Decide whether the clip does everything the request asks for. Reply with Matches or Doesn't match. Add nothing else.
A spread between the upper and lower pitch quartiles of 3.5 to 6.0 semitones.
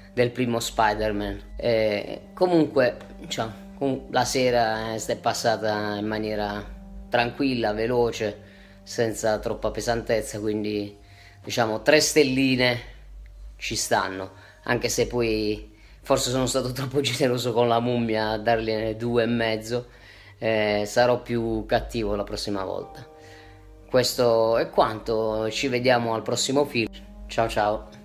Doesn't match